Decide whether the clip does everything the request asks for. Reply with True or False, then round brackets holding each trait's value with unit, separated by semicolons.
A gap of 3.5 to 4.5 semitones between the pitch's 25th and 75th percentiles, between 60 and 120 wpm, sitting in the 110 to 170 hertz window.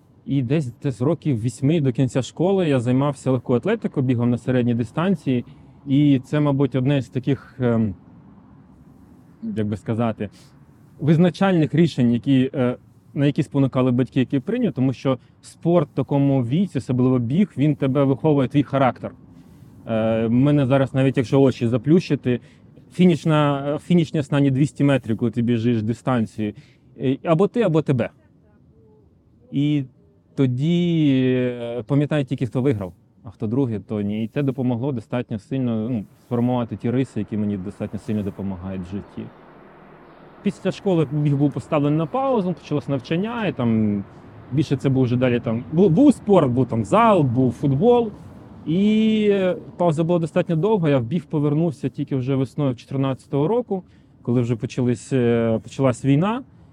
False (3.8 semitones; 145 wpm; 135 Hz)